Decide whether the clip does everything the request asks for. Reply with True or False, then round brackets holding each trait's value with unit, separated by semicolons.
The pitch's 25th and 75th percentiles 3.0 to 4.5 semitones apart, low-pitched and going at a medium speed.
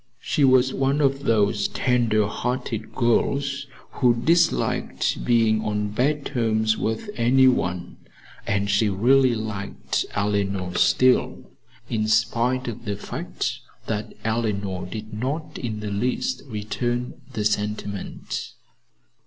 False (3.6 semitones; 115 Hz; 120 wpm)